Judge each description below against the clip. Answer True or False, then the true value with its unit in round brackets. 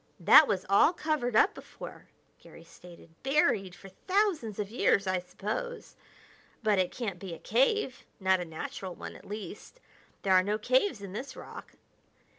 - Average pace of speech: True (165 wpm)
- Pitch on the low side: False (210 Hz)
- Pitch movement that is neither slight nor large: False (6.0 semitones)